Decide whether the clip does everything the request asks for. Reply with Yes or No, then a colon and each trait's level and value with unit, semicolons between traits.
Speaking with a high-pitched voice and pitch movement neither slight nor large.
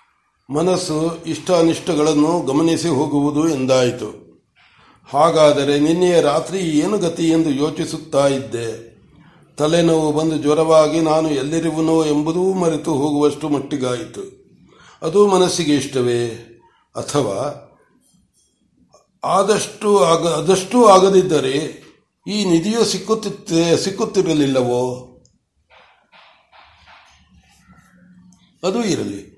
No: medium, 160 Hz; average, 3.5 semitones